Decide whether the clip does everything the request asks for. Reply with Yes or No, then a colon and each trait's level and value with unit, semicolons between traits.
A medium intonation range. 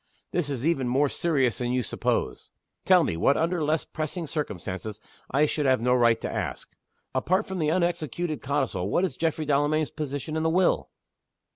Yes: average, 4.3 semitones